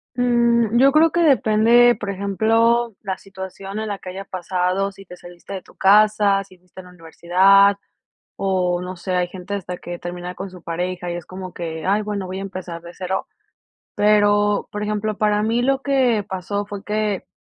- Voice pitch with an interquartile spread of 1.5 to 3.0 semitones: Yes, average, 2.7 semitones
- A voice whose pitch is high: Yes, high, 195 Hz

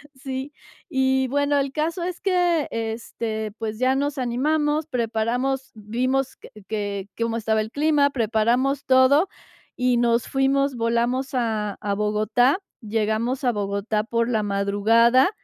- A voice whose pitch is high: Yes, high, 245 Hz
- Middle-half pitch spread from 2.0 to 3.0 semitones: No, average, 3.7 semitones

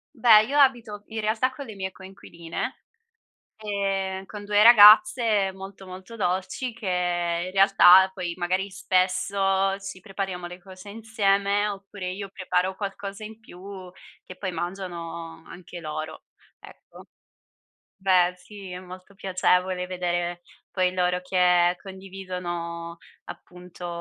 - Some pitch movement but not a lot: No, narrow, 1.9 semitones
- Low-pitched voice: No, high, 190 Hz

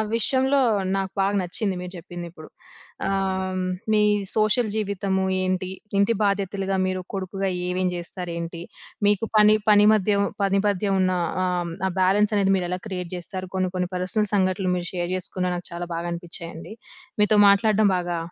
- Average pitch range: No, narrow, 2.0 semitones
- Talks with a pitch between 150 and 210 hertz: Yes, high, 190 Hz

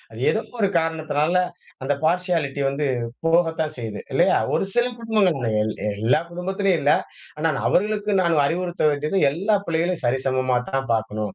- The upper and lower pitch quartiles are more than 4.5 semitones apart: Yes, average, 5.1 semitones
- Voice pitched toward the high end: No, medium, 160 Hz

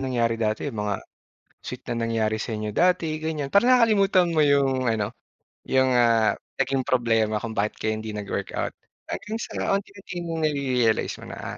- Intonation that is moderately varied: No, wide, 6.5 semitones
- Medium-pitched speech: No, low, 130 Hz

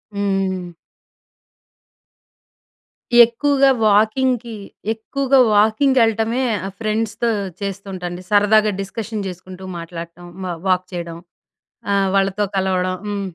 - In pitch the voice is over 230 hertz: No, high, 200 Hz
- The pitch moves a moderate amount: Yes, average, 3.2 semitones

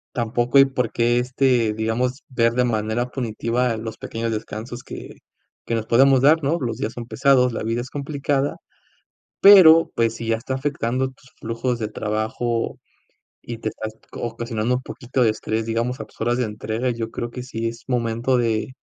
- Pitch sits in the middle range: No, low, 120 Hz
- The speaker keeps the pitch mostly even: Yes, narrow, 2.2 semitones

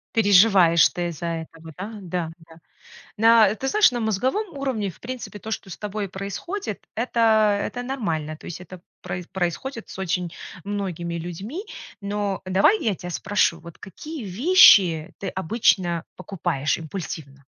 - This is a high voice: Yes, high, 195 Hz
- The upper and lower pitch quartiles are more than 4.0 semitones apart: Yes, average, 4.7 semitones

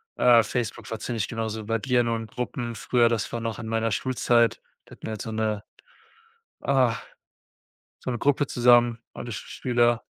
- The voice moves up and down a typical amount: No, narrow, 1.5 semitones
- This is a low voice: Yes, low, 115 Hz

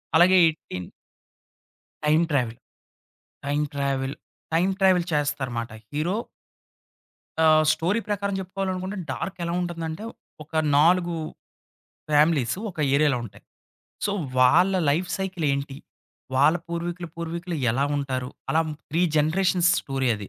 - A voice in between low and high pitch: Yes, medium, 160 Hz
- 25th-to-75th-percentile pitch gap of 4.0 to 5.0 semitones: Yes, average, 4.3 semitones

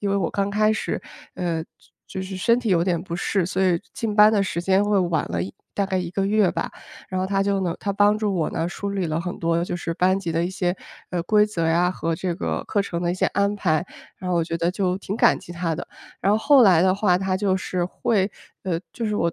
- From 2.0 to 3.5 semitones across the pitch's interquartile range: Yes, average, 2.7 semitones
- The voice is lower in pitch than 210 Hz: Yes, medium, 185 Hz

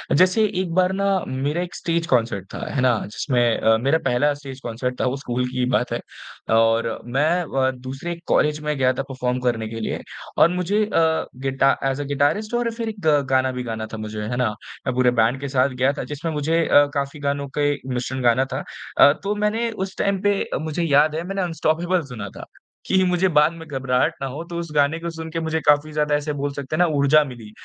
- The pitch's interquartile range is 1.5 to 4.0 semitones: No, average, 4.7 semitones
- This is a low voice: No, medium, 145 Hz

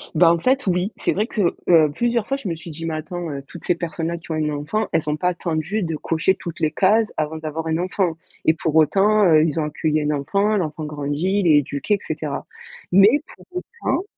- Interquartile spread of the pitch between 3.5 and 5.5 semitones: Yes, average, 4.0 semitones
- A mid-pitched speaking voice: Yes, medium, 165 Hz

